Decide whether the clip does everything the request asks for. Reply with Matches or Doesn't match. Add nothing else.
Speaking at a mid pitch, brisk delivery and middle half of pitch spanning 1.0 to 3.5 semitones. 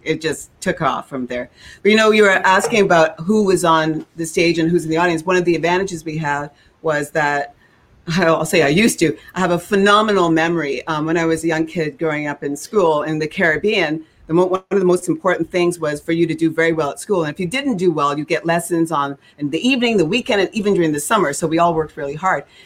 Matches